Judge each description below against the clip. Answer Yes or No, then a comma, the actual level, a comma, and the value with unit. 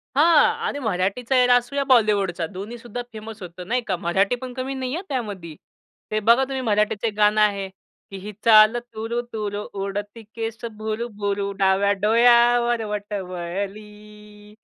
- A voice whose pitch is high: Yes, high, 215 Hz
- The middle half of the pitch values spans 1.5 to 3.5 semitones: Yes, average, 3.0 semitones